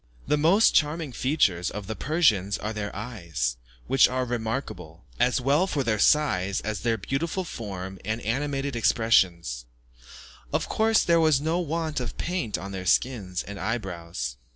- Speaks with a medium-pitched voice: No, low, 115 Hz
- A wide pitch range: Yes, wide, 7.3 semitones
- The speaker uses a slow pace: No, average, 160 wpm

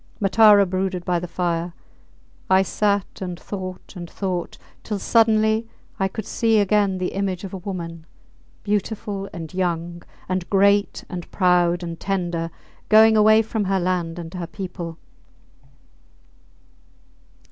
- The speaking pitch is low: No, high, 190 Hz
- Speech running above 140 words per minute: No, slow, 135 wpm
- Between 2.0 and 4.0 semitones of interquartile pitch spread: Yes, narrow, 2.6 semitones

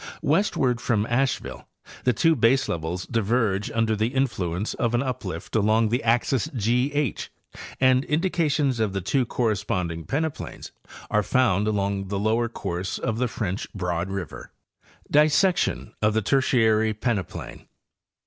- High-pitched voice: No, low, 115 Hz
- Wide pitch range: No, average, 4.3 semitones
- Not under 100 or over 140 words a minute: Yes, slow, 135 wpm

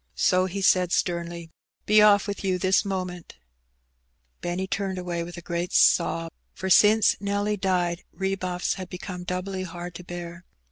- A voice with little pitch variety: Yes, narrow, 1.9 semitones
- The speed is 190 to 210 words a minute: No, average, 160 wpm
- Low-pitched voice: No, medium, 180 Hz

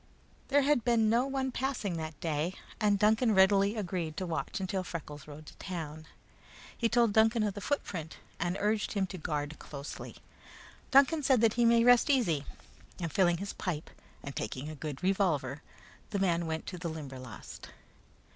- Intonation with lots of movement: Yes, wide, 6.1 semitones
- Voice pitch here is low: No, high, 190 Hz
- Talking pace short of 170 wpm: No, average, 175 wpm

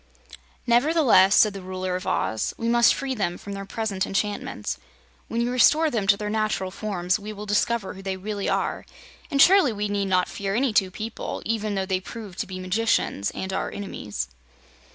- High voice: Yes, high, 205 Hz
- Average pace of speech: Yes, average, 195 wpm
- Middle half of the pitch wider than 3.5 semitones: No, average, 3.2 semitones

